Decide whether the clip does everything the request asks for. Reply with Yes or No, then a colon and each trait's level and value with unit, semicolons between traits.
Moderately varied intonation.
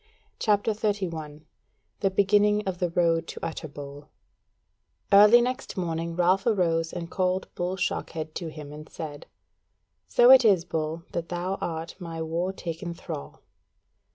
Yes: average, 3.2 semitones